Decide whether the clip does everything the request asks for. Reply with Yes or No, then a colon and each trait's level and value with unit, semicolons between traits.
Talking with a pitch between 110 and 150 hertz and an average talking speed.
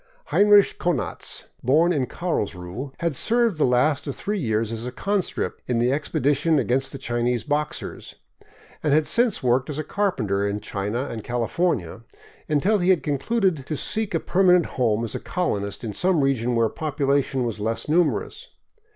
Yes: medium, 140 Hz; average, 170 wpm